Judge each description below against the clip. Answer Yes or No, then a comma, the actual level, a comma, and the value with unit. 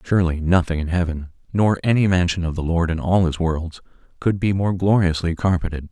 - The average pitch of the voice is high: No, very low, 90 Hz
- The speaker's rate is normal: Yes, average, 195 wpm